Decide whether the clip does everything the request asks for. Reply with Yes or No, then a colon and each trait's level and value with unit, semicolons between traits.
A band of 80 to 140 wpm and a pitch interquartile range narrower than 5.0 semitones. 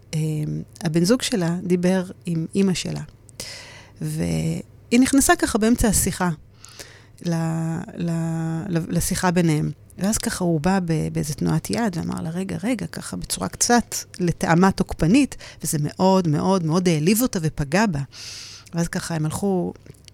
Yes: average, 135 wpm; average, 4.0 semitones